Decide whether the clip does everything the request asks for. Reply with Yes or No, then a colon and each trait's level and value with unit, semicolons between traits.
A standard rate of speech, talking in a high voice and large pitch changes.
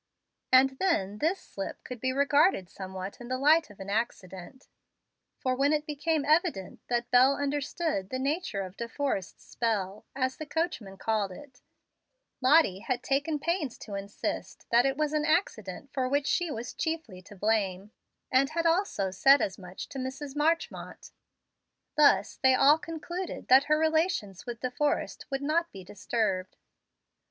Yes: average, 165 wpm; very high, 260 Hz; wide, 6.7 semitones